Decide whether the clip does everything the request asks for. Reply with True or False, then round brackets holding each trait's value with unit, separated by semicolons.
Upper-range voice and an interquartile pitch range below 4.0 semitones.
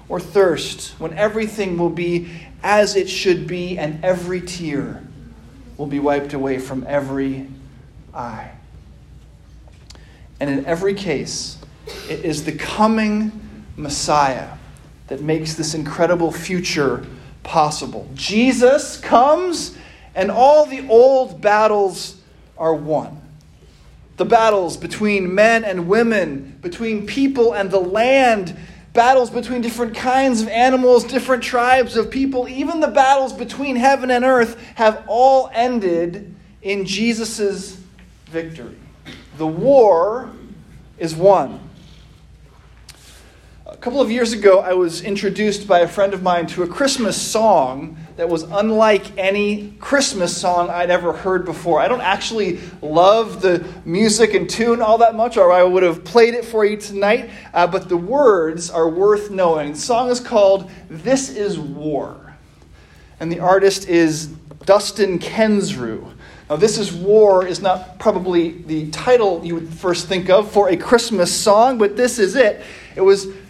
False (195 Hz; 4.8 semitones)